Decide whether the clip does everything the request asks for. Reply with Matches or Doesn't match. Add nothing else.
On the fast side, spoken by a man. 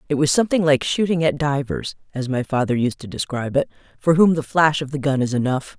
Doesn't match